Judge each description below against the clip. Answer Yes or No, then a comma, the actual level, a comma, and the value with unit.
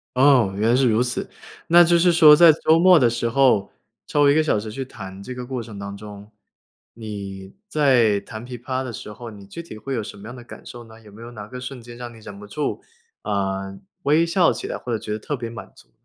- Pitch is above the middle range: No, low, 120 Hz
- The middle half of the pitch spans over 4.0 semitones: Yes, average, 4.5 semitones